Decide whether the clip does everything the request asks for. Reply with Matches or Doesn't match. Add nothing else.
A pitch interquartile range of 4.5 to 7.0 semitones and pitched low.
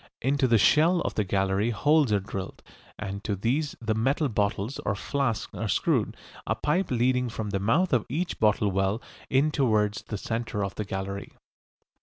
Matches